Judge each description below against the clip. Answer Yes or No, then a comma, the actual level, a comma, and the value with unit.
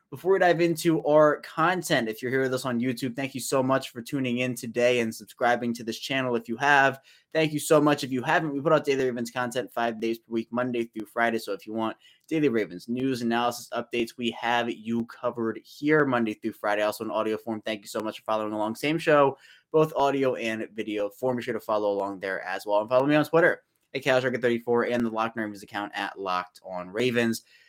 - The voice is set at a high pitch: No, low, 120 Hz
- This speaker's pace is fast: Yes, fast, 230 wpm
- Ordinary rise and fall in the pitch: Yes, average, 3.5 semitones